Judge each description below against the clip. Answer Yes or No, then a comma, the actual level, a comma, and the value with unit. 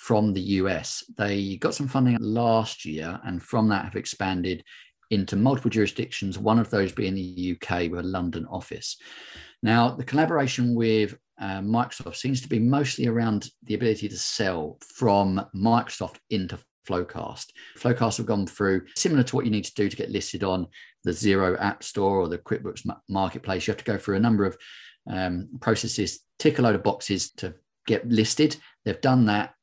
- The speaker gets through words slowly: No, average, 180 wpm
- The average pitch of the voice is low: Yes, low, 105 Hz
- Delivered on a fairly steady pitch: No, average, 3.4 semitones